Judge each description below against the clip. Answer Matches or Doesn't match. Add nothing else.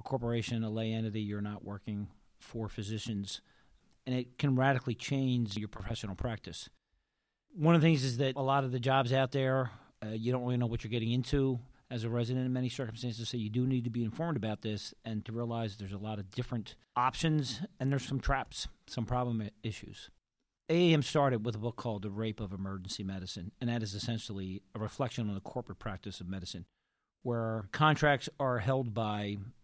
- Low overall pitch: Matches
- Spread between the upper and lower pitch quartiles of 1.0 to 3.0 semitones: Doesn't match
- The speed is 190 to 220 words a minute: Matches